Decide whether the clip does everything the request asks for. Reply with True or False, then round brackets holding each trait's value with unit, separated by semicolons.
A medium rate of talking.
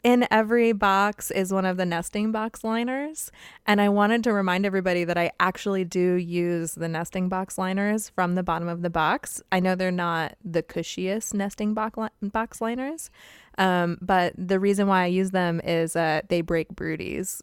True (195 wpm)